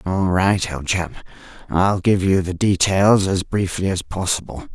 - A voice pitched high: No, very low, 95 Hz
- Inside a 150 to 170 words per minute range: Yes, average, 165 wpm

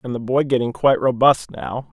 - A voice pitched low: Yes, low, 125 Hz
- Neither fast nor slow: No, fast, 210 wpm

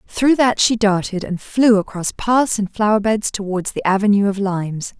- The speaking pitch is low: No, high, 205 Hz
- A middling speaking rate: Yes, average, 180 wpm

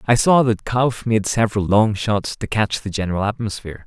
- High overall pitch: No, low, 105 Hz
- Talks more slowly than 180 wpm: No, average, 200 wpm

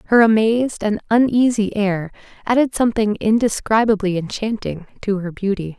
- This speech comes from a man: No, female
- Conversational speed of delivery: No, slow, 125 wpm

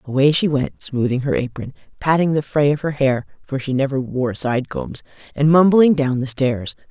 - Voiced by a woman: Yes, female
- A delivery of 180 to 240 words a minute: Yes, average, 185 wpm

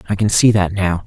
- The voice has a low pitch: Yes, very low, 95 Hz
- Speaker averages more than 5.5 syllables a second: Yes, 5.8 syllables/s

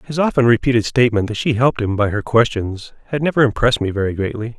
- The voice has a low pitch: Yes, low, 120 Hz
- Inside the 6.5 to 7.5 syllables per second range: Yes, 6.8 syllables/s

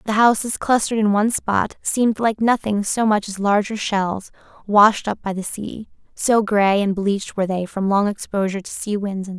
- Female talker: Yes, female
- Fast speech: Yes, fast, 210 wpm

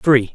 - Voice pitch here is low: Yes, low, 120 Hz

